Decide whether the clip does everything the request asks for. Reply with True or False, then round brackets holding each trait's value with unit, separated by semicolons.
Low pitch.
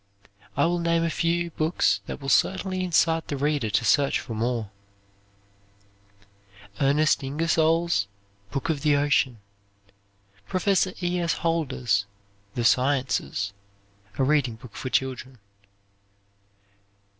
False (145 Hz)